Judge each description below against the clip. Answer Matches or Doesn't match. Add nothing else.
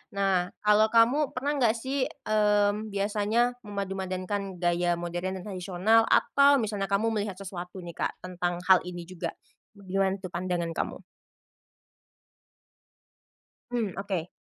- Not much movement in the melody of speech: Doesn't match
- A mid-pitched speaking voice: Doesn't match